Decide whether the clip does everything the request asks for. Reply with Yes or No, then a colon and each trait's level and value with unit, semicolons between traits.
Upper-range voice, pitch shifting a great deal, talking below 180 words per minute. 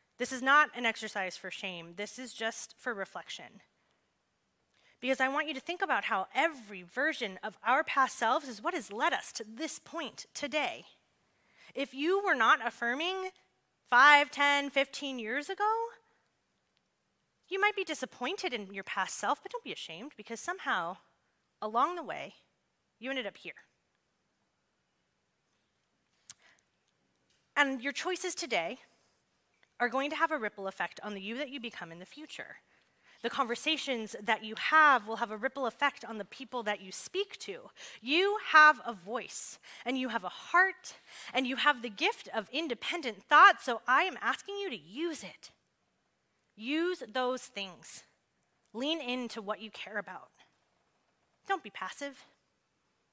Yes: very high, 265 Hz; wide, 5.8 semitones; average, 160 wpm